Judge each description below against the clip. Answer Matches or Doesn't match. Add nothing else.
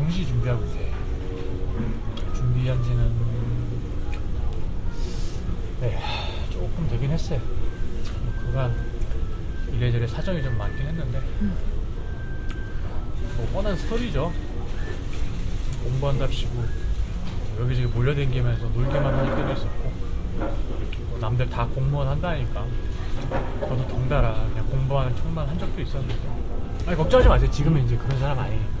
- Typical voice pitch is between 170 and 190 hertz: Doesn't match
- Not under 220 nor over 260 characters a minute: Matches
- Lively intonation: Doesn't match